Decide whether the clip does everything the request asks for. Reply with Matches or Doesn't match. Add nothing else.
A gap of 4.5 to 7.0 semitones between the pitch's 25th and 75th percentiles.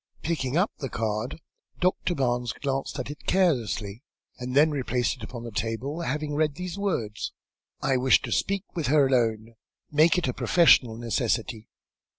Matches